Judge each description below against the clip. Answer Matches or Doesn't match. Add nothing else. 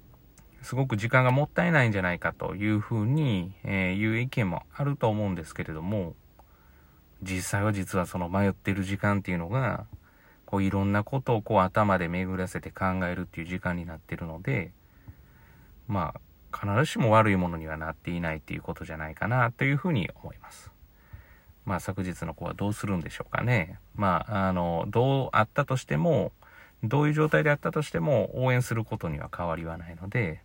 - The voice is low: Matches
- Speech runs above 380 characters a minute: Matches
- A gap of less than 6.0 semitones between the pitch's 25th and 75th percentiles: Matches